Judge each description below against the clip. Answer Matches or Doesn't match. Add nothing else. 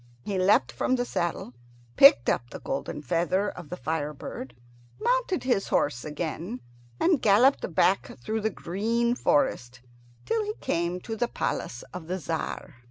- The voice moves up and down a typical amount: Doesn't match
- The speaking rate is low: Doesn't match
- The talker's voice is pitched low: Doesn't match